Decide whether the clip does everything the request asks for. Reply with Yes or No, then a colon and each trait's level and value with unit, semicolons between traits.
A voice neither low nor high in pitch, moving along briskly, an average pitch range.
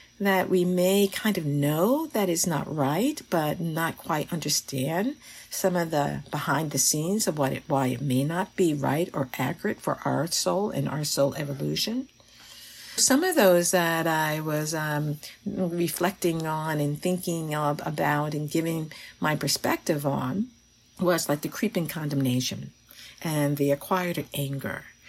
No: medium, 160 Hz; average, 155 wpm; average, 4.0 semitones